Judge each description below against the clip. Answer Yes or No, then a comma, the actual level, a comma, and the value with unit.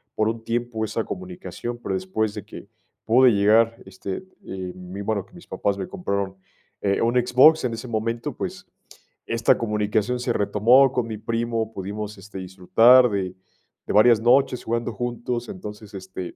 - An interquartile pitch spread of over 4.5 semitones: No, average, 3.2 semitones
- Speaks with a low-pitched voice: Yes, low, 110 Hz